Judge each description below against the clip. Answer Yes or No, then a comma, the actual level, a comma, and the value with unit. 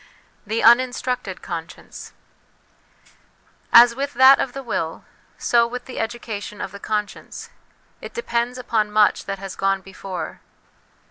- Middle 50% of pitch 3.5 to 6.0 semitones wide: Yes, average, 3.9 semitones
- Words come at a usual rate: No, slow, 130 wpm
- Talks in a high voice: Yes, high, 230 Hz